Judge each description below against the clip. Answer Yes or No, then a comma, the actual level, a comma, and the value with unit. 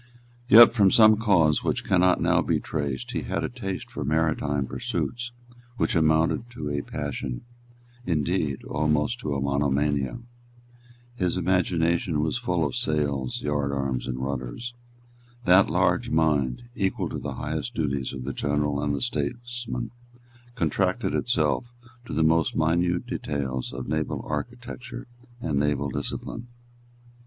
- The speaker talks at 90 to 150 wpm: Yes, slow, 135 wpm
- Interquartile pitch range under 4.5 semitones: No, average, 4.8 semitones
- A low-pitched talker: Yes, very low, 75 Hz